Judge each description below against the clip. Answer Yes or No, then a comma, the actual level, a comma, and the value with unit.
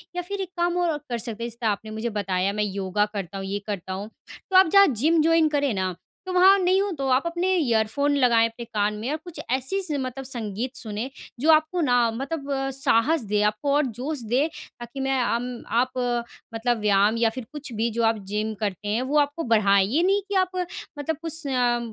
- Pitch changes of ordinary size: No, wide, 6.1 semitones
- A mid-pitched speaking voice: No, very high, 250 Hz